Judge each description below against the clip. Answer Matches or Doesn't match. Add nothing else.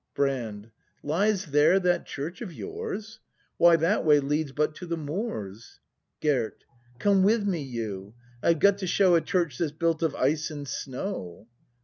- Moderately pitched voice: Matches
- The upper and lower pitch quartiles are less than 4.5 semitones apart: Doesn't match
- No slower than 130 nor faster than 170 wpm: Matches